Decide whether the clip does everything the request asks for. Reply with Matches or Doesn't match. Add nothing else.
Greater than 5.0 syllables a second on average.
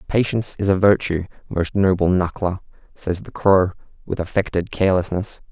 Matches